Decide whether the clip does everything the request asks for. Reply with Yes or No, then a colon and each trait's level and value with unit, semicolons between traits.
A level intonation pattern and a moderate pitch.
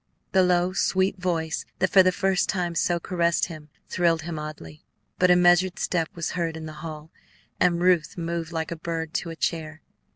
Yes: narrow, 1.9 semitones; medium, 170 Hz